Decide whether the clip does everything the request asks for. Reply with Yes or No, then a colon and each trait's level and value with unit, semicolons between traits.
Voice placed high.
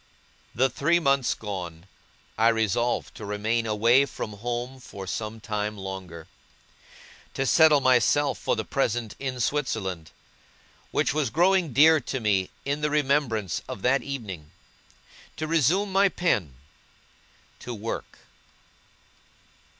No: low, 120 Hz